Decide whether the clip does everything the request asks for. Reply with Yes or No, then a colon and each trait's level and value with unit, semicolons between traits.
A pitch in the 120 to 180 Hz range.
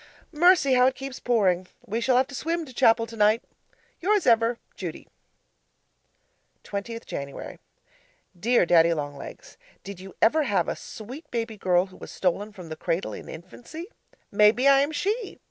No: high, 230 Hz